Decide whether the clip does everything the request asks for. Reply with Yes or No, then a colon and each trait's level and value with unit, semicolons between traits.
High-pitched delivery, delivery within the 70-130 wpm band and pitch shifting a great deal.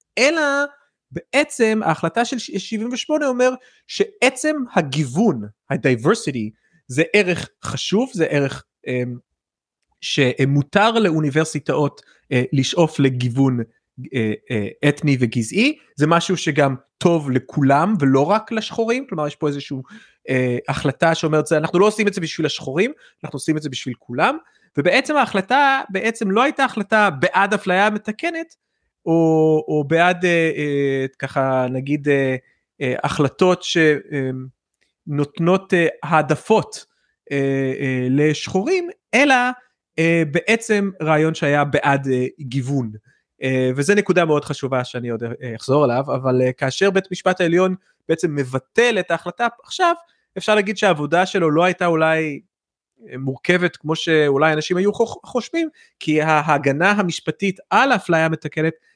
No: medium, 160 Hz; average, 115 wpm; wide, 6.9 semitones